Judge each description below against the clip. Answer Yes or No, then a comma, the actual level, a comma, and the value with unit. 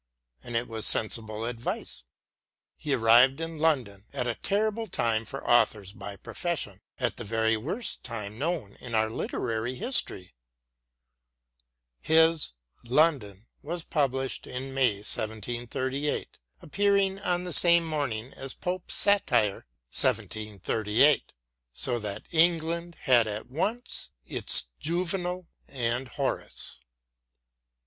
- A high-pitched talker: No, low, 130 Hz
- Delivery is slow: Yes, slow, 120 wpm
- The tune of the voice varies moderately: No, wide, 6.8 semitones